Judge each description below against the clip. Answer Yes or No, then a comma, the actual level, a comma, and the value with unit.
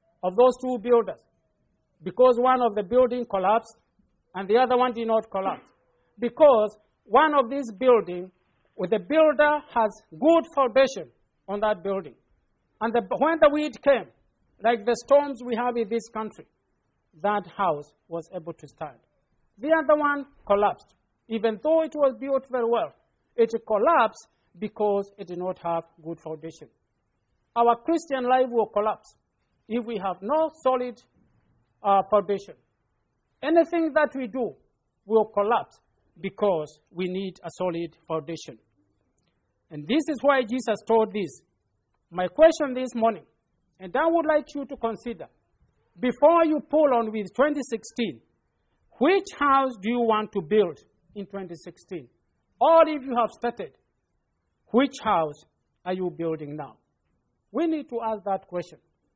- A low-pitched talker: No, high, 225 Hz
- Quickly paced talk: No, average, 150 wpm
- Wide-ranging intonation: Yes, wide, 6.2 semitones